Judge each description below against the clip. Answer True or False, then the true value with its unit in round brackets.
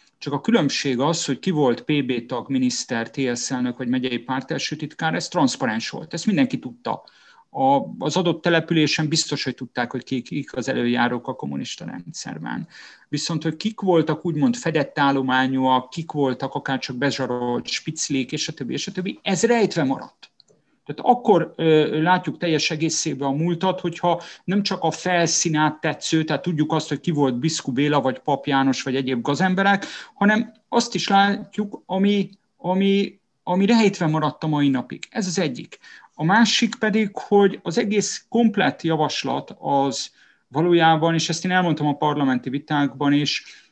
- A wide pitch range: True (5.8 semitones)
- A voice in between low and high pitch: True (160 Hz)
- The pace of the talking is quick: True (165 wpm)